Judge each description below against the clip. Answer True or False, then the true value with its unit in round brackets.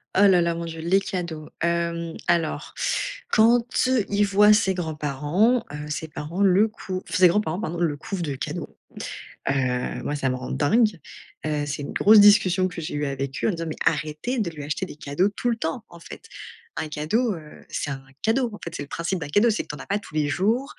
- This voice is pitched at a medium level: True (170 Hz)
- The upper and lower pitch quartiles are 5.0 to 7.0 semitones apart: True (5.3 semitones)